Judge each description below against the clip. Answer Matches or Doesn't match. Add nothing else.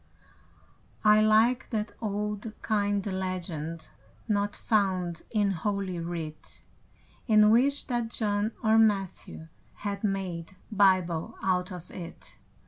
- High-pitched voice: Matches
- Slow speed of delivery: Matches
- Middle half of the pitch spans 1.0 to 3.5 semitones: Matches